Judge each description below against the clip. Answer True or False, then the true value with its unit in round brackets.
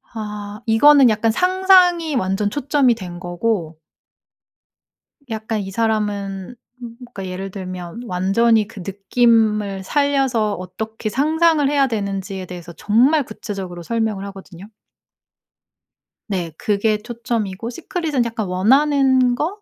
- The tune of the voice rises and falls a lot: False (4.5 semitones)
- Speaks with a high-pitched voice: True (220 Hz)